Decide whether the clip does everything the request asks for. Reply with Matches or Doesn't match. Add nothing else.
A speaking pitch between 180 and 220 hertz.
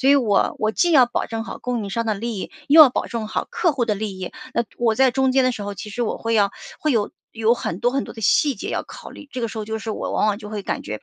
Doesn't match